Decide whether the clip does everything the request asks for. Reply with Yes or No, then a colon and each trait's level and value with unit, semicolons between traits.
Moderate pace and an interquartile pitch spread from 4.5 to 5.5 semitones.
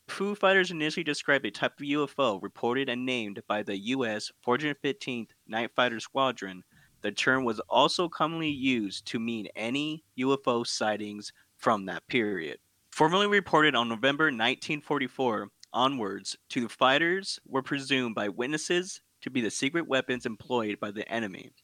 Yes: average, 155 wpm; average, 5.0 semitones